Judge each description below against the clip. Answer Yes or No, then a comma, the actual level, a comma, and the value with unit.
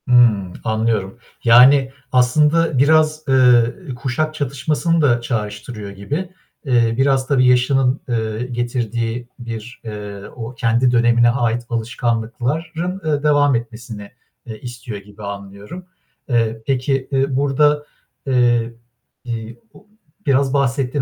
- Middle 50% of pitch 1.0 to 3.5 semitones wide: Yes, average, 3.1 semitones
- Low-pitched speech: Yes, low, 125 Hz